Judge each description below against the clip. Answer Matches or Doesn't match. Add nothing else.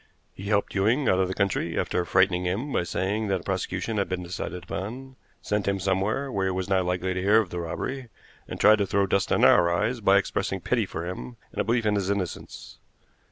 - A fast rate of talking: Matches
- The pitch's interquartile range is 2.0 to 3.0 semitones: Matches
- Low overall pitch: Matches